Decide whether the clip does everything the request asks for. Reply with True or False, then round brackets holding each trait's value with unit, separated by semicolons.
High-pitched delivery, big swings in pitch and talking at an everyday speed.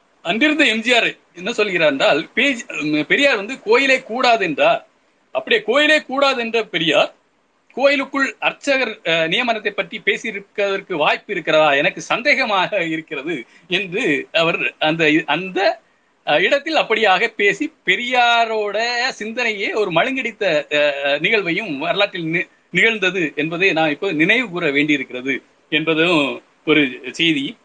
True (225 Hz; 9.0 semitones; 100 wpm)